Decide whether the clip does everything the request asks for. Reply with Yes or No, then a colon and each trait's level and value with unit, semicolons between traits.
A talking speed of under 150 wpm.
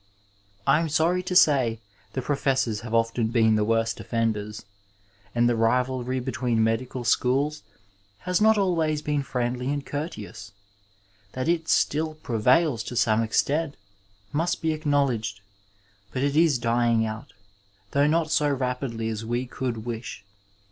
Yes: average, 140 wpm